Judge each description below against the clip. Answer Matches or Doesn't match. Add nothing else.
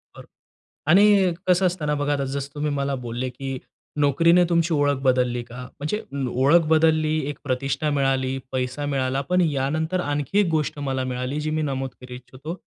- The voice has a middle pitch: Matches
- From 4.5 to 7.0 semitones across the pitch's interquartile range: Doesn't match